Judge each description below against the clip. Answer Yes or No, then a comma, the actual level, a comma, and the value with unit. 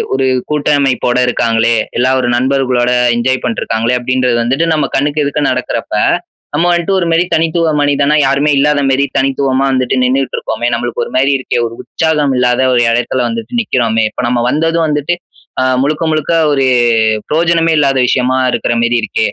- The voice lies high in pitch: No, low, 135 Hz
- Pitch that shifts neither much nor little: Yes, average, 3.4 semitones